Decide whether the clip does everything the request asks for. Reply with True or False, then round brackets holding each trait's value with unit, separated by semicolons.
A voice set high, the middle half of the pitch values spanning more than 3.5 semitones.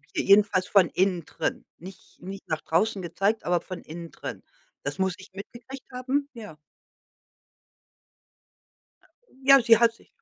True (195 Hz; 4.5 semitones)